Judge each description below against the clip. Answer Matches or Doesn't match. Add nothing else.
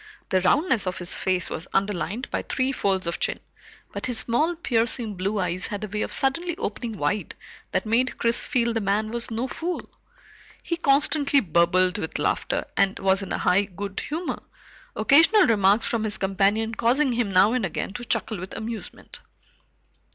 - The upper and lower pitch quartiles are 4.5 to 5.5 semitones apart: Matches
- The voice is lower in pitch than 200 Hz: Doesn't match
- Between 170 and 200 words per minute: Matches